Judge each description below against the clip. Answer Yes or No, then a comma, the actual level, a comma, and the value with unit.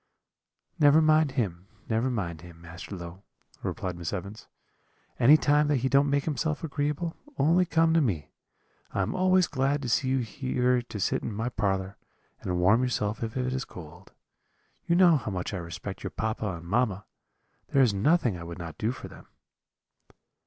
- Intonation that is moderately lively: No, wide, 7.2 semitones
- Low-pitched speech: Yes, low, 120 Hz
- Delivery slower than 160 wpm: No, average, 180 wpm